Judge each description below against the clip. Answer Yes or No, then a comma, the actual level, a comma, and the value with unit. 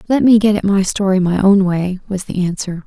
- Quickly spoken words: Yes, fast, 230 wpm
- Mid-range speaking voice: No, high, 195 Hz